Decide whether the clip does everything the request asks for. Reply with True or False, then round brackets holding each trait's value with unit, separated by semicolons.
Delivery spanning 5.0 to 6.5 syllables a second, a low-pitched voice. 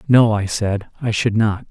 False (4.4 syllables/s; 110 Hz)